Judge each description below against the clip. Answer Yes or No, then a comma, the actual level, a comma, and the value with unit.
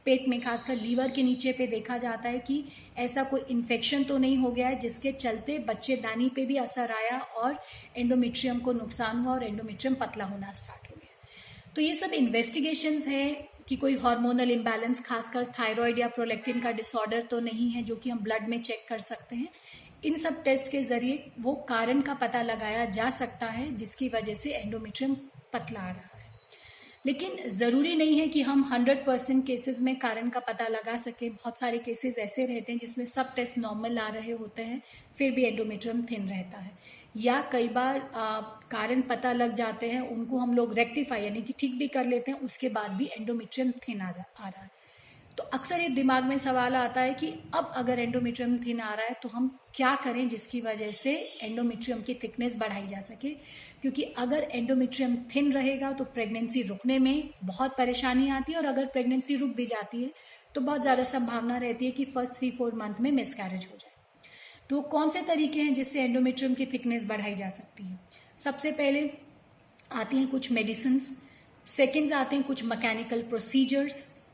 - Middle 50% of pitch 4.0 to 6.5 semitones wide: No, narrow, 2.5 semitones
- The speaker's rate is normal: No, fast, 195 wpm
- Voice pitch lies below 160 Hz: No, high, 245 Hz